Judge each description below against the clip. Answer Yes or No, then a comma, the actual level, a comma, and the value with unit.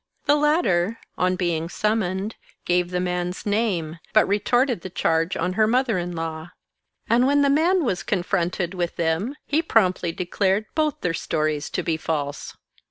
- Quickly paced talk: No, average, 165 wpm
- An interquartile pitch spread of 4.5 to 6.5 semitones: Yes, average, 4.9 semitones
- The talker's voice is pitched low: No, medium, 185 Hz